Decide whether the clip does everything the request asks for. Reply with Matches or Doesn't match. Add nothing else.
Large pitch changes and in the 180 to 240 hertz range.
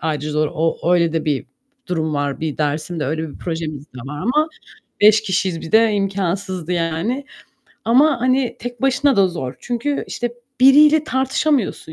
Matches